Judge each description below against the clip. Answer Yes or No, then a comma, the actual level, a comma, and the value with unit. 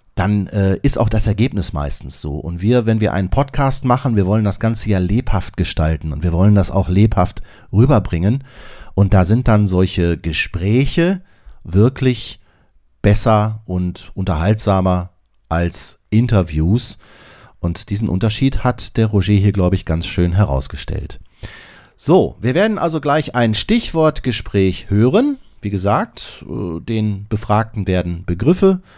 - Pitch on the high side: No, low, 105 Hz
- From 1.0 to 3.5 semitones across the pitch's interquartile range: No, average, 4.2 semitones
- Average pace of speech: Yes, average, 140 wpm